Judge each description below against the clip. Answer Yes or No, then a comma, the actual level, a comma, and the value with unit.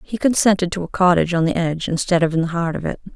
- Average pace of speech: No, fast, 285 wpm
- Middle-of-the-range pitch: Yes, medium, 175 Hz